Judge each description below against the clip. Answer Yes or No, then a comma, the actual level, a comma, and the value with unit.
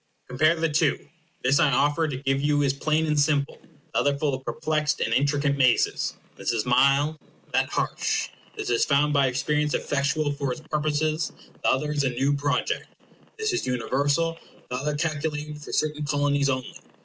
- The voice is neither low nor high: Yes, medium, 145 Hz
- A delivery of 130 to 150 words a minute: No, average, 180 wpm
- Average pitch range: No, narrow, 1.8 semitones